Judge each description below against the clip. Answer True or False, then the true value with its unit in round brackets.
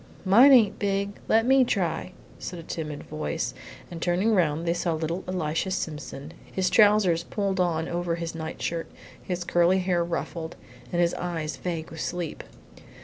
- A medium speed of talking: True (160 wpm)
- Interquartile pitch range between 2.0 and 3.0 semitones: True (2.5 semitones)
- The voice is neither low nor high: True (175 Hz)